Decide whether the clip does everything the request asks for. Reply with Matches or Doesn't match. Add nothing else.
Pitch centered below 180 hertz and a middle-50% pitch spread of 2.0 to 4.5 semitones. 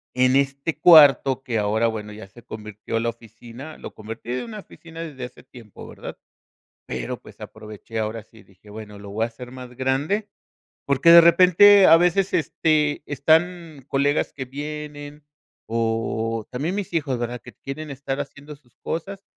Doesn't match